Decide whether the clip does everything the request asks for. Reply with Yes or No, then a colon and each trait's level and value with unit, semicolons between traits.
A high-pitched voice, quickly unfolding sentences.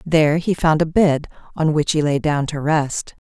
No: medium, 155 Hz; fast, 220 wpm